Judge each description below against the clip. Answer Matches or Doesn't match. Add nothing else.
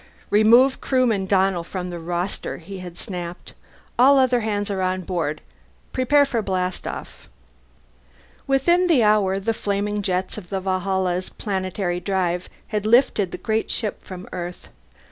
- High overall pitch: Matches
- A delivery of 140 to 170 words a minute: Matches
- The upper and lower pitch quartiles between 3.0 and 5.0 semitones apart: Matches